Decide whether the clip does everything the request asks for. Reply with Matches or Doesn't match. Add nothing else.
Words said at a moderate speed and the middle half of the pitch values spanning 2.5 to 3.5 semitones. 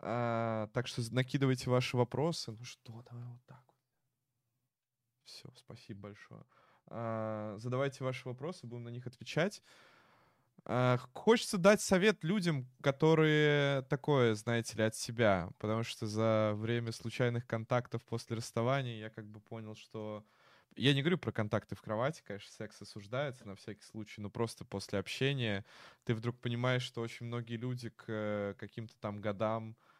Matches